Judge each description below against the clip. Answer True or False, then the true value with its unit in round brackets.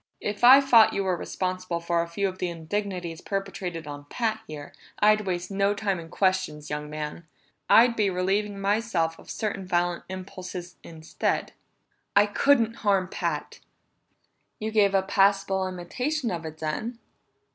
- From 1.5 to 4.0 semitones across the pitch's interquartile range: True (3.4 semitones)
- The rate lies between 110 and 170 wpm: True (155 wpm)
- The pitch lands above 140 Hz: True (190 Hz)